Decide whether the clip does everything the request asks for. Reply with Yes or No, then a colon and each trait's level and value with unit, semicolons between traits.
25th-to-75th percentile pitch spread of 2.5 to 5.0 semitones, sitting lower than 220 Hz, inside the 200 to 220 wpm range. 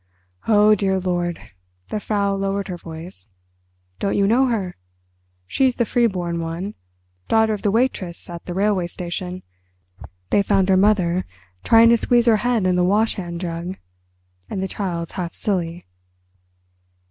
No: average, 3.6 semitones; medium, 185 Hz; average, 145 wpm